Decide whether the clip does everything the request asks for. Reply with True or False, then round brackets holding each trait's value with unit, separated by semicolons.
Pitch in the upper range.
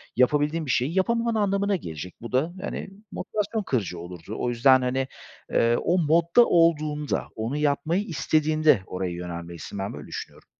False (145 Hz)